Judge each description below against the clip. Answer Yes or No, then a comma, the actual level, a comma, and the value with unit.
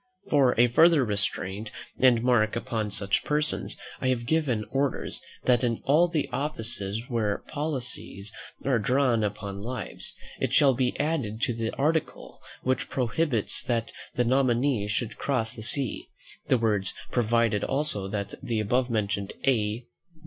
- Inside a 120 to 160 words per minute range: Yes, average, 145 wpm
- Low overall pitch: Yes, low, 120 Hz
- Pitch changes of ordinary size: Yes, average, 3.9 semitones